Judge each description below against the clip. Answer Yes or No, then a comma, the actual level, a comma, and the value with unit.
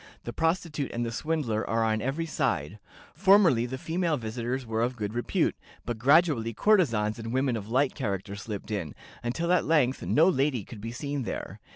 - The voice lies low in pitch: Yes, low, 125 Hz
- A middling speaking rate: Yes, average, 185 wpm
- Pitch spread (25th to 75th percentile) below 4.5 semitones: No, average, 5.3 semitones